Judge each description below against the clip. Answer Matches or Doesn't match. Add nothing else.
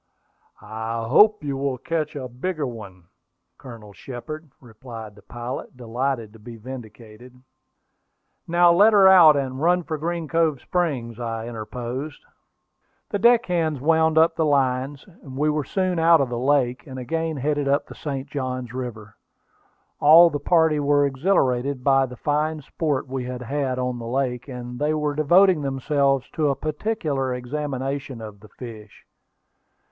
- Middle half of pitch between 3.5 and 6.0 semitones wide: Matches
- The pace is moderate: Matches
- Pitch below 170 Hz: Matches